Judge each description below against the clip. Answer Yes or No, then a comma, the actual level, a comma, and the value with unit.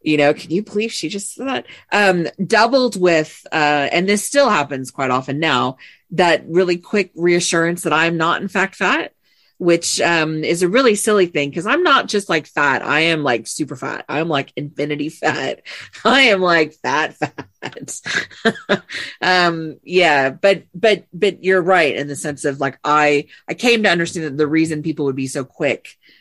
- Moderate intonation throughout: Yes, average, 4.4 semitones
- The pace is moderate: Yes, average, 190 wpm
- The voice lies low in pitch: No, medium, 170 Hz